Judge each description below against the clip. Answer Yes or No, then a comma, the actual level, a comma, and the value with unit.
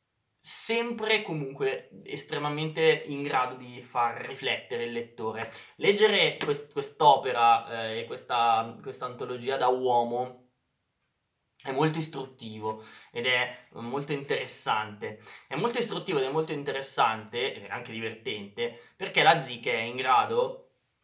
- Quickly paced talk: No, average, 120 wpm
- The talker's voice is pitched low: Yes, low, 130 Hz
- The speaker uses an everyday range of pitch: No, wide, 5.7 semitones